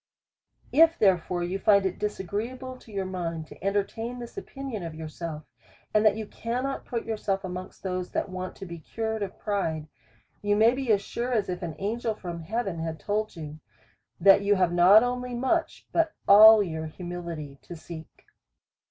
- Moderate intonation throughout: Yes, average, 4.4 semitones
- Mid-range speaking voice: No, high, 200 Hz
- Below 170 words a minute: No, average, 180 wpm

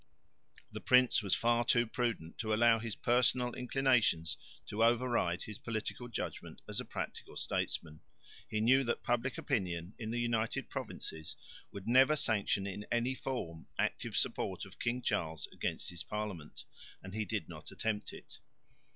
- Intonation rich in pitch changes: No, average, 3.6 semitones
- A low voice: Yes, low, 115 Hz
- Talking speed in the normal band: Yes, average, 155 wpm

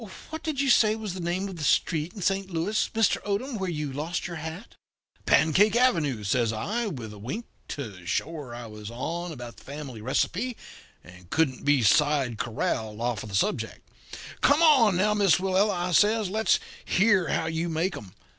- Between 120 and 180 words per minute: No, average, 195 wpm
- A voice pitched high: No, medium, 165 Hz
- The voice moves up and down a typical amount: No, wide, 8.3 semitones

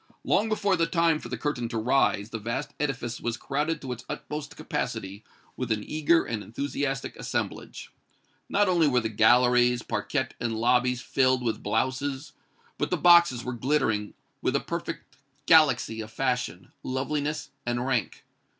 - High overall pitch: No, low, 125 Hz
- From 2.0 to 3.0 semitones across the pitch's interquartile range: No, average, 4.1 semitones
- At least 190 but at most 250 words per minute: No, average, 160 wpm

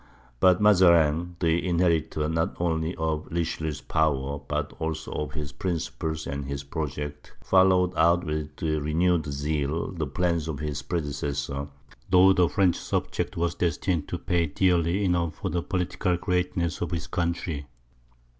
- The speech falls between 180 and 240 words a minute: No, average, 145 wpm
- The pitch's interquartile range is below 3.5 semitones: Yes, average, 2.9 semitones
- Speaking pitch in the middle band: No, very low, 80 Hz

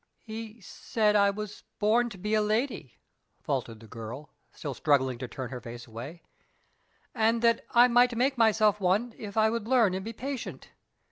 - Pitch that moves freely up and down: Yes, wide, 8.1 semitones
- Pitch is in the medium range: No, high, 210 Hz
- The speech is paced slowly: No, average, 180 wpm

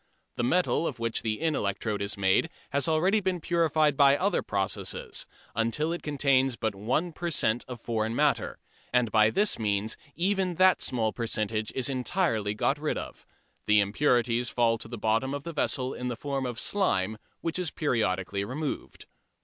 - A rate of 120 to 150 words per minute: No, average, 175 wpm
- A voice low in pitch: Yes, low, 125 Hz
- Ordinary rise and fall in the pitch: No, wide, 6.1 semitones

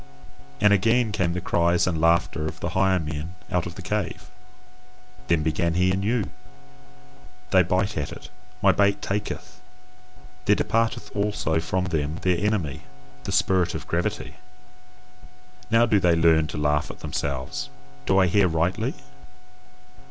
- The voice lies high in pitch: No, very low, 90 Hz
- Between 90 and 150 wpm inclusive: Yes, average, 145 wpm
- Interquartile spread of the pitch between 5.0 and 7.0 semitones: No, average, 3.6 semitones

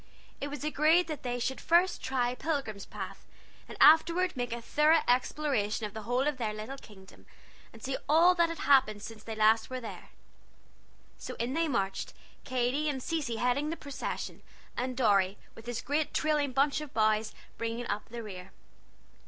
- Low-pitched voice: No, very high, 255 Hz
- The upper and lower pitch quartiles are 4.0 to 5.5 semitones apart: Yes, average, 5.1 semitones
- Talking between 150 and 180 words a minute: Yes, average, 175 wpm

